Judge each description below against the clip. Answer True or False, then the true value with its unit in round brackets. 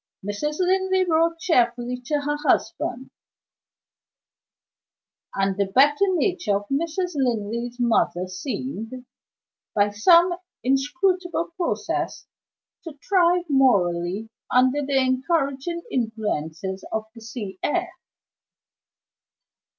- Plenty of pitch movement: True (7.5 semitones)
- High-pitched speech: True (260 Hz)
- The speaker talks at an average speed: False (95 wpm)